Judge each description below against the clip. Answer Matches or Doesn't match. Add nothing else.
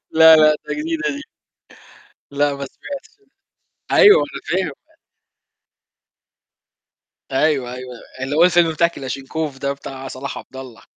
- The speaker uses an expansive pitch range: Doesn't match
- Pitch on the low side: Doesn't match